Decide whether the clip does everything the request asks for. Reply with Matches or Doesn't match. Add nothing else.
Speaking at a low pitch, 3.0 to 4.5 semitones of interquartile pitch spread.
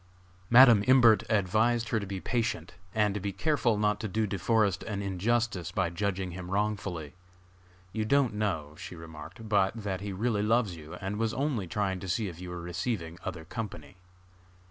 Matches